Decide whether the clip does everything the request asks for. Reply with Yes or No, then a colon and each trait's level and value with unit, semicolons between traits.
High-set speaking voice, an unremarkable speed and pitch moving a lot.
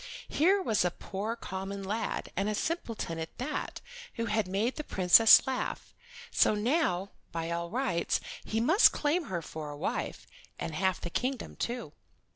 Yes: high, 210 Hz; average, 175 wpm; wide, 5.9 semitones